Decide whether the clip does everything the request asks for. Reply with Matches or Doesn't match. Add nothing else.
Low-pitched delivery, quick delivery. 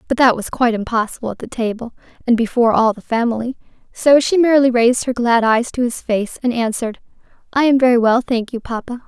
Doesn't match